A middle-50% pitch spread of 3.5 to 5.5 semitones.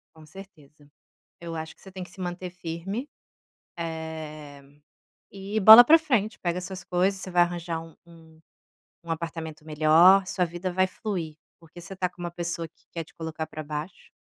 No: average, 2.7 semitones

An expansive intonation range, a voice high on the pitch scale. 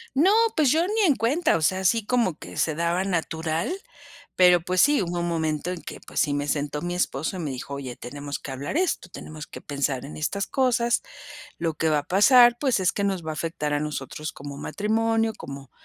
No: wide, 7.0 semitones; medium, 170 Hz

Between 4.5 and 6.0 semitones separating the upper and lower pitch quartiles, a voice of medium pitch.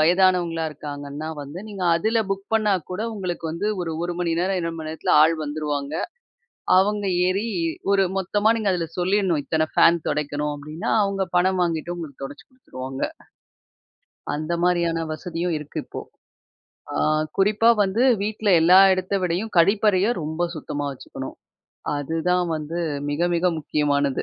No: average, 3.8 semitones; medium, 170 Hz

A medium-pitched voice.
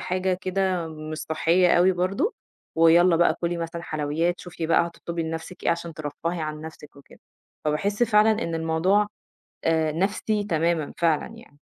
Yes: medium, 170 Hz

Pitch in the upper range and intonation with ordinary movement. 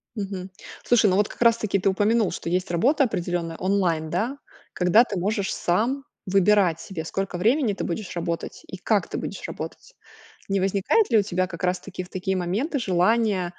Yes: high, 195 Hz; average, 3.4 semitones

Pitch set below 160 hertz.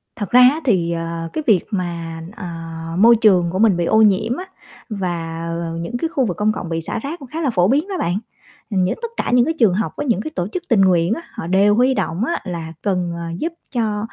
No: high, 200 Hz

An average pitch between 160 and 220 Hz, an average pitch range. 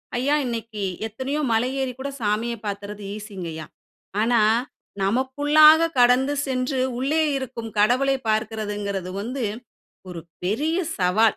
No: high, 235 Hz; average, 4.2 semitones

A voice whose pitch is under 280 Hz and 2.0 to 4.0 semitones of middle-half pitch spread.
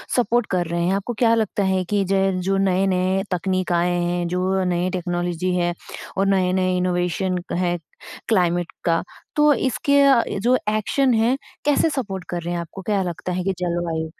Yes: medium, 185 Hz; narrow, 2.4 semitones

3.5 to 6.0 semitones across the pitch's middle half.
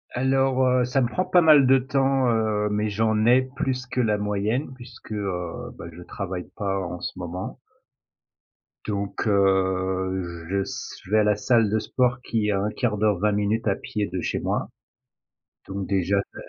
Yes: average, 4.3 semitones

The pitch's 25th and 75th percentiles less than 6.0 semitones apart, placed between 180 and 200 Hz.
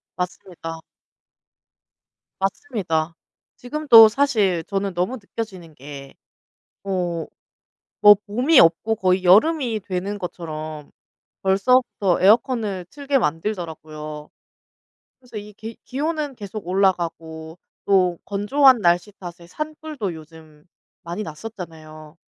Yes: average, 5.3 semitones; high, 190 Hz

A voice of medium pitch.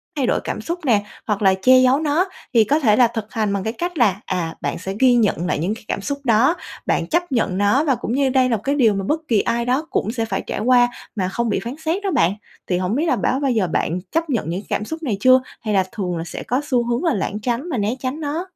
No: high, 235 Hz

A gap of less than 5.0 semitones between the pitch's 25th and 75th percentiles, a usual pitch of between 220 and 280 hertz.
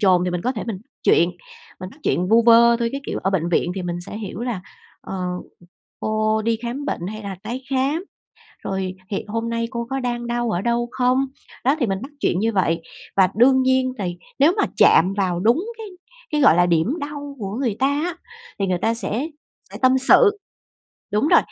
No: average, 5.3 semitones; high, 230 Hz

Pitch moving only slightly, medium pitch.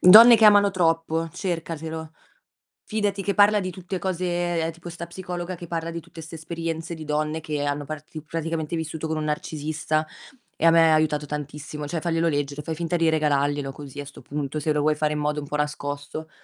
Yes: narrow, 2.3 semitones; medium, 160 Hz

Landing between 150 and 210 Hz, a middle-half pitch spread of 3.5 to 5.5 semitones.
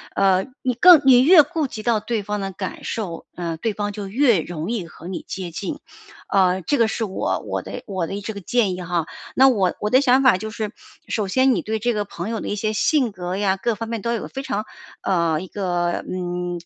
Yes: high, 205 Hz; average, 4.3 semitones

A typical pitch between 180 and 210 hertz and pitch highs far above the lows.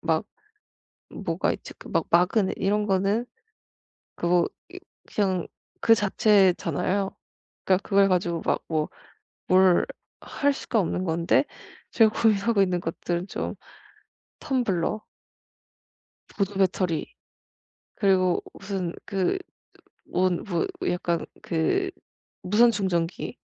No: high, 190 Hz; average, 2.9 semitones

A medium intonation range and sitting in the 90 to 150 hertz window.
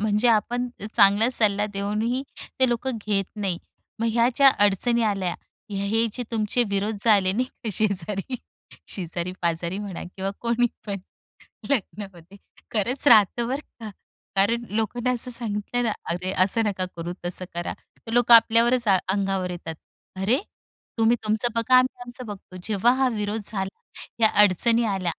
No: average, 3.4 semitones; high, 210 Hz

